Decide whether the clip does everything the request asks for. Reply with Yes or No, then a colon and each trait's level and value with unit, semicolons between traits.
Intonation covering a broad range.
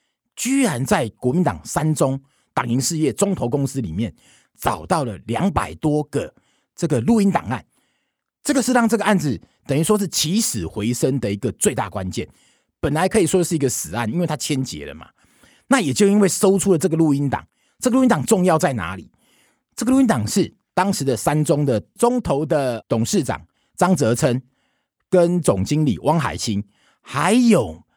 Yes: wide, 7.4 semitones